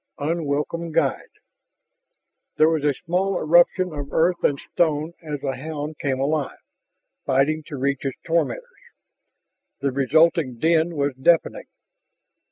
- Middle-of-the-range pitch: Yes, medium, 155 Hz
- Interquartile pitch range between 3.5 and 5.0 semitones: No, average, 3.0 semitones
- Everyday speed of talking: No, slow, 130 wpm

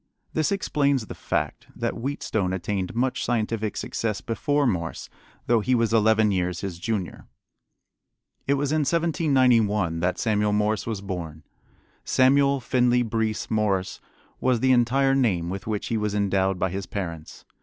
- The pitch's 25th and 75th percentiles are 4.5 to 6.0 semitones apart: Yes, average, 4.9 semitones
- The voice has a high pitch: No, low, 110 Hz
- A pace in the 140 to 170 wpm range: Yes, average, 150 wpm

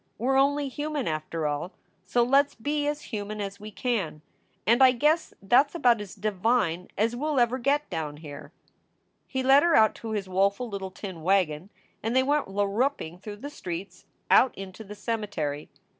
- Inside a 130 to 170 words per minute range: No, average, 190 wpm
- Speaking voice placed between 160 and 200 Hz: No, high, 215 Hz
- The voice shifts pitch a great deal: Yes, wide, 5.9 semitones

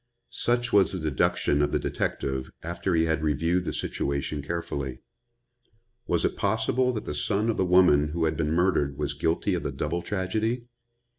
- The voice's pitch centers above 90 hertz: No, very low, 85 Hz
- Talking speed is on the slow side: No, average, 175 wpm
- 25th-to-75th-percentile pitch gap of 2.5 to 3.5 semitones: No, average, 4.7 semitones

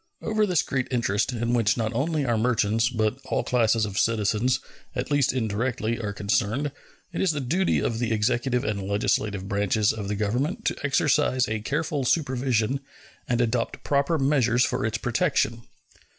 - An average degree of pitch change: Yes, average, 4.0 semitones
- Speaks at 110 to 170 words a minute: Yes, average, 165 wpm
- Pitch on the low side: Yes, low, 120 Hz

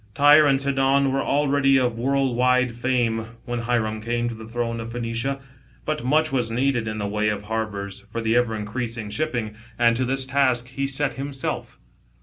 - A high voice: No, low, 120 Hz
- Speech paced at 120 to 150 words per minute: No, average, 185 wpm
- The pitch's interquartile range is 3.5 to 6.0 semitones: No, average, 3.1 semitones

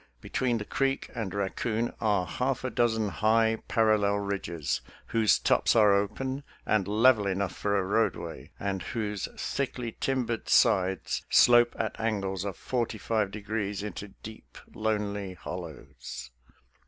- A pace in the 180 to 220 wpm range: No, average, 140 wpm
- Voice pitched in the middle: No, low, 105 Hz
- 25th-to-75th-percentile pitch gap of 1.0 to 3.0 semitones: Yes, narrow, 2.5 semitones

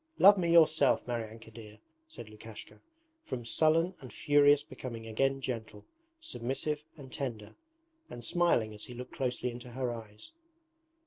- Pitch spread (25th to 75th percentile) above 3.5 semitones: Yes, average, 4.3 semitones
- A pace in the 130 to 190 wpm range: Yes, average, 140 wpm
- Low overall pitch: Yes, low, 125 Hz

